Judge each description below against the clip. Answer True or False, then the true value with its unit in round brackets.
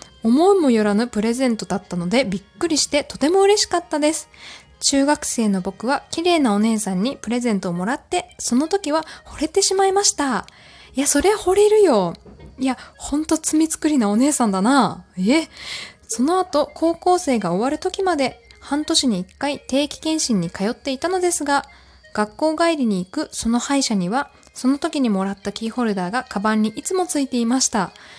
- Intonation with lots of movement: True (6.1 semitones)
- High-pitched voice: True (275 Hz)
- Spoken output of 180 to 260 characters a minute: False (360 characters per minute)